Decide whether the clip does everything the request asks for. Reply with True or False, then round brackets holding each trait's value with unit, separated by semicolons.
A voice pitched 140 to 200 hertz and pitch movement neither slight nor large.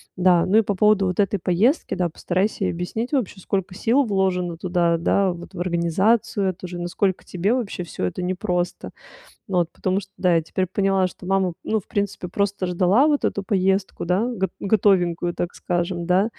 False (185 Hz; 2.2 semitones)